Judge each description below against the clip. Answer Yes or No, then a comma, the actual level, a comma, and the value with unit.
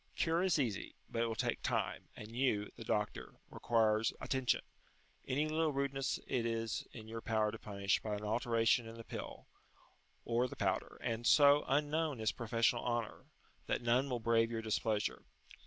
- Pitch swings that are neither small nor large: Yes, average, 3.1 semitones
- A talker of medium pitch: No, low, 115 Hz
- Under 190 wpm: Yes, average, 170 wpm